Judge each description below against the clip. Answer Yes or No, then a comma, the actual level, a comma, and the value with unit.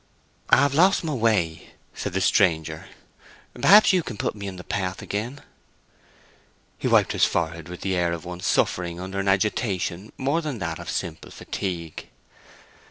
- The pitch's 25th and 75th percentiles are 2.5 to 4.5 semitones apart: No, average, 5.1 semitones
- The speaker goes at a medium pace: Yes, average, 165 wpm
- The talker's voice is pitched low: Yes, very low, 95 Hz